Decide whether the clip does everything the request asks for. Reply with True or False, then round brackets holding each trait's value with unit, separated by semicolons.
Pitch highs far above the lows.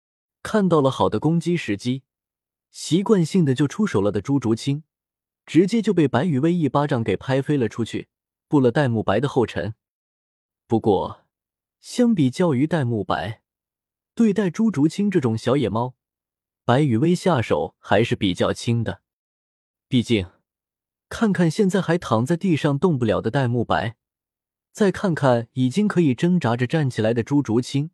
True (7.3 semitones)